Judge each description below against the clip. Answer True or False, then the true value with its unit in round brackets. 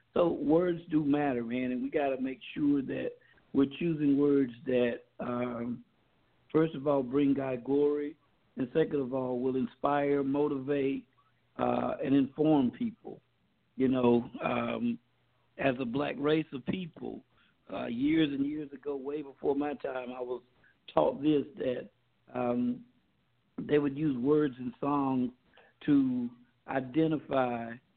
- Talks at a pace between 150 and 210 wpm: False (140 wpm)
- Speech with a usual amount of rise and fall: True (3.1 semitones)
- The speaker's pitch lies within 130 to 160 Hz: True (140 Hz)